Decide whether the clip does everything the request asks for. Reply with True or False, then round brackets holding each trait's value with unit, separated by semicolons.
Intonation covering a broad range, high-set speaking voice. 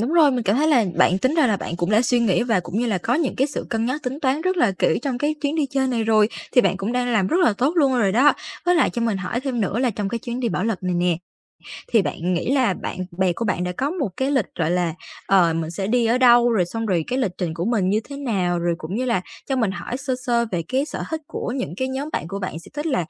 True (5.7 semitones; 235 Hz)